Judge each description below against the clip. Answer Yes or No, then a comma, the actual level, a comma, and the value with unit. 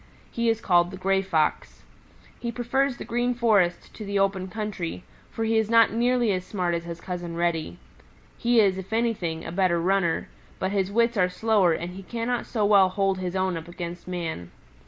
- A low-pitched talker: No, high, 195 Hz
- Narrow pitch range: No, average, 4.3 semitones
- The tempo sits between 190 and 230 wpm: Yes, average, 195 wpm